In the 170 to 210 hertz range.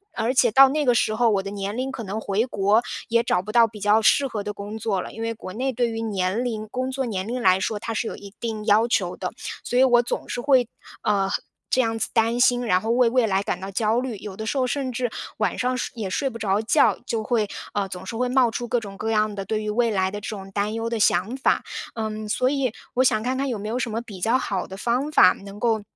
No: high, 225 Hz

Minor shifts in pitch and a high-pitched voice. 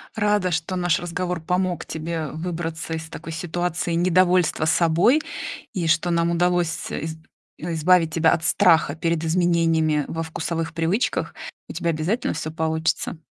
No: narrow, 1.7 semitones; medium, 165 Hz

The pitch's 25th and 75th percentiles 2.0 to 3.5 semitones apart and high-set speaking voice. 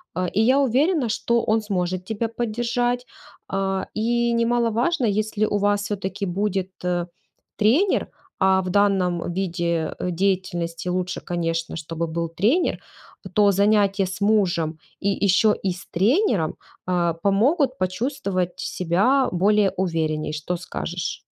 No: average, 4.0 semitones; high, 195 Hz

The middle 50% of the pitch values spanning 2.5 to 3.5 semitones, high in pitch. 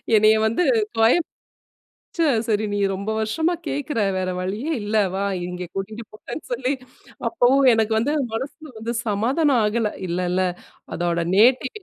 No: average, 4.6 semitones; high, 225 Hz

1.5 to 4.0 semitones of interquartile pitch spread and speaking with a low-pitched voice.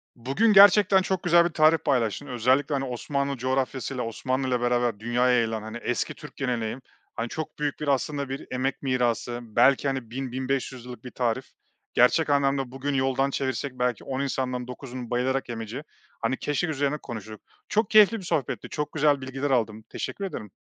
Yes: average, 2.7 semitones; low, 130 Hz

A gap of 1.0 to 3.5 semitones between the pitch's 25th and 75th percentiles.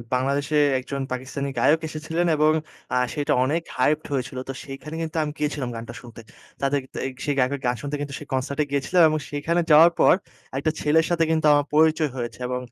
Yes: average, 2.8 semitones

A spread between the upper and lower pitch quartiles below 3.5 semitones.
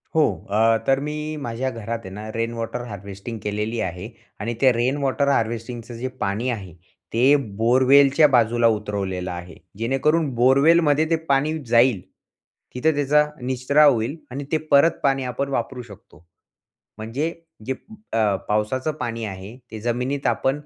No: average, 4.0 semitones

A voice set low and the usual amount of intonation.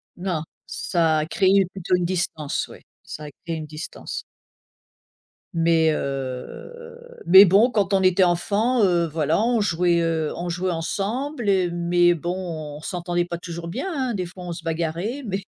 No: medium, 175 Hz; average, 3.1 semitones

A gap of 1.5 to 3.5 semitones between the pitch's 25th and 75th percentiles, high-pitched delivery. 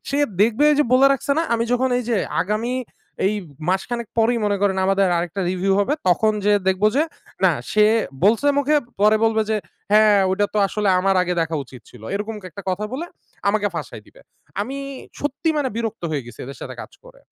No: average, 4.1 semitones; high, 210 Hz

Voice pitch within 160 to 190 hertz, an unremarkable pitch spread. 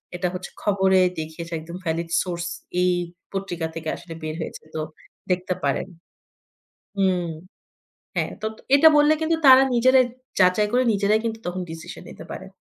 Yes: medium, 185 Hz; average, 4.2 semitones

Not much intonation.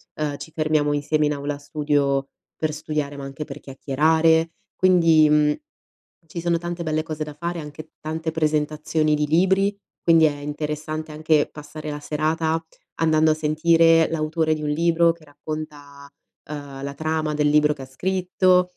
Yes: narrow, 1.6 semitones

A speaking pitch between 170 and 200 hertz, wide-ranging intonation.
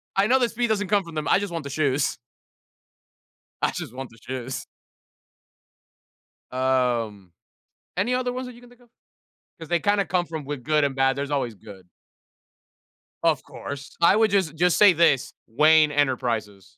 No: medium, 150 Hz; wide, 7.0 semitones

